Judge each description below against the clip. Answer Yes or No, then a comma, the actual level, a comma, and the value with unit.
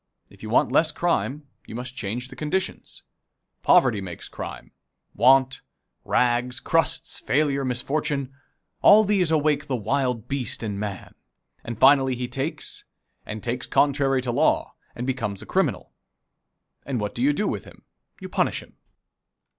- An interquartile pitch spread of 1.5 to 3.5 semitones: Yes, average, 3.0 semitones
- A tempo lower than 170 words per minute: Yes, average, 150 wpm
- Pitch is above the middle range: No, low, 130 Hz